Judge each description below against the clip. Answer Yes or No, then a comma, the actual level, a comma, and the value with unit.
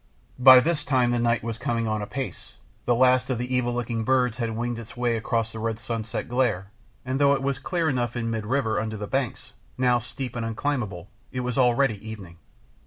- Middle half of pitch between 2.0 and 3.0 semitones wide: Yes, narrow, 2.4 semitones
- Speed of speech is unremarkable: No, fast, 210 wpm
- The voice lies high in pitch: No, low, 120 Hz